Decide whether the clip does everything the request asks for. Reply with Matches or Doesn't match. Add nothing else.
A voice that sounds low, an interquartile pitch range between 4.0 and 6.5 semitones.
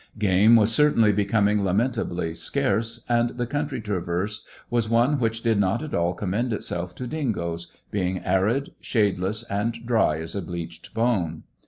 Matches